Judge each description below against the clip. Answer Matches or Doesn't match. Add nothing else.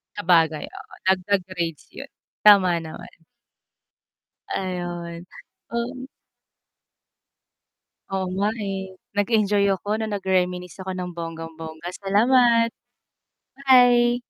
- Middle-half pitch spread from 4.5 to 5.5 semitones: Doesn't match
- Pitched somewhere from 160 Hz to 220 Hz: Matches